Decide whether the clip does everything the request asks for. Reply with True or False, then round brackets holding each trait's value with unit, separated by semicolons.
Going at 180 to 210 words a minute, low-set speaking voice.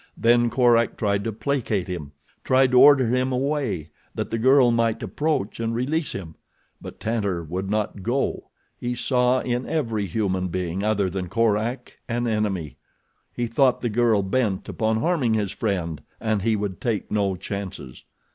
False (165 wpm; 110 Hz)